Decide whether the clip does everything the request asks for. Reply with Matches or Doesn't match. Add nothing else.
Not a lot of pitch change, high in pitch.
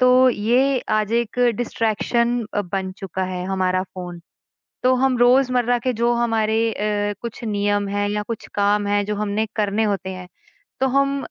Doesn't match